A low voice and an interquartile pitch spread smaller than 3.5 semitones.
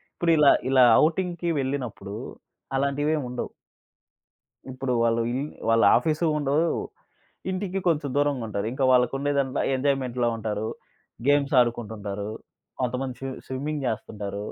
No: low, 130 Hz; average, 3.8 semitones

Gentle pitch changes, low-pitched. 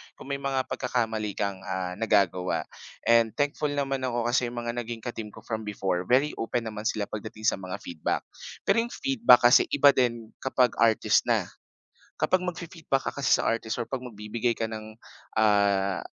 No: average, 3.7 semitones; low, 115 Hz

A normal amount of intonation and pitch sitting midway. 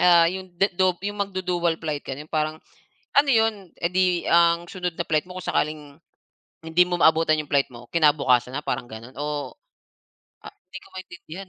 Yes: average, 3.3 semitones; medium, 170 Hz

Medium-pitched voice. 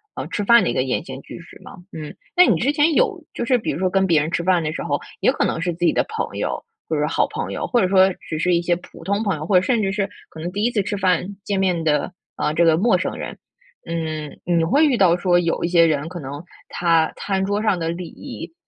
Yes: medium, 180 Hz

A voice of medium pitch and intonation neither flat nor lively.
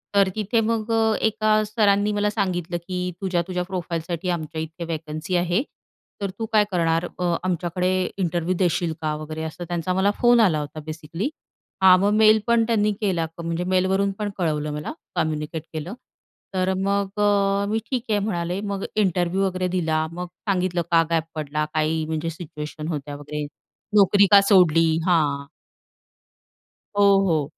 Yes: medium, 180 Hz; average, 3.8 semitones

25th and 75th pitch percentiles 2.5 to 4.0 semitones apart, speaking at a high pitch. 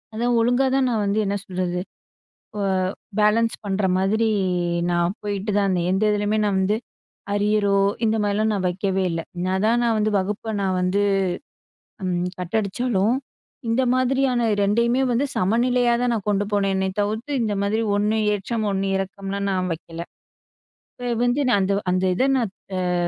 Yes: average, 3.0 semitones; high, 205 Hz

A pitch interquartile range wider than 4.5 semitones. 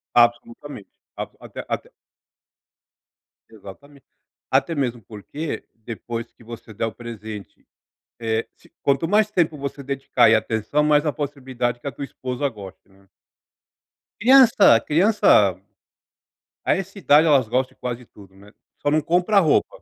Yes: average, 4.9 semitones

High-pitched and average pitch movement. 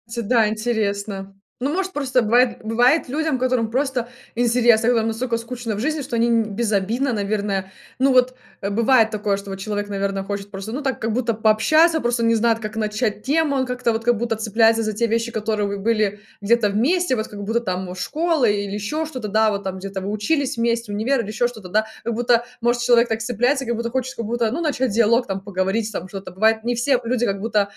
Yes: high, 230 Hz; average, 3.0 semitones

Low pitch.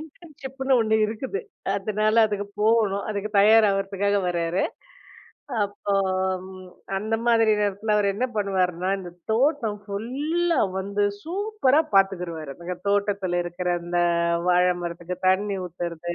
No: high, 200 Hz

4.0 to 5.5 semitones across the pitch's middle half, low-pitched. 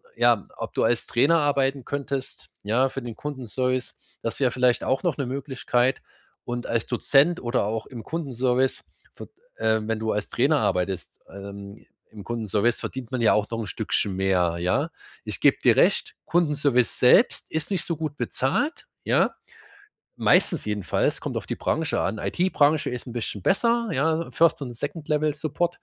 Yes: average, 4.9 semitones; low, 130 Hz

